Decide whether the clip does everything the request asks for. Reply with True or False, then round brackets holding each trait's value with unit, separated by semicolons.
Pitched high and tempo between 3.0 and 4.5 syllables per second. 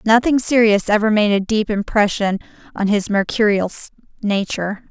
False (210 Hz; 5.2 syllables/s)